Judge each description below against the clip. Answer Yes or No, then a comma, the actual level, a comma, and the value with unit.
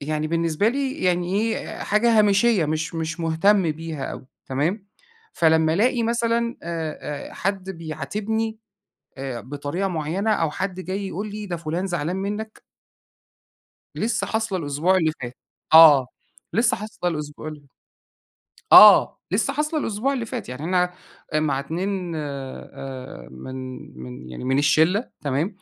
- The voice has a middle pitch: Yes, medium, 170 Hz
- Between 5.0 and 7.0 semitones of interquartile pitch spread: Yes, wide, 5.4 semitones